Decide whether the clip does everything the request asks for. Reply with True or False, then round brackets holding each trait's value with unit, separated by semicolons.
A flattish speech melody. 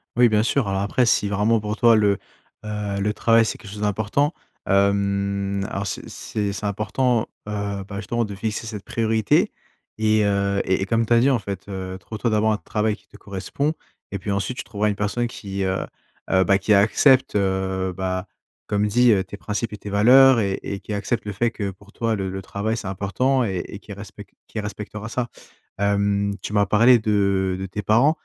True (2.0 semitones)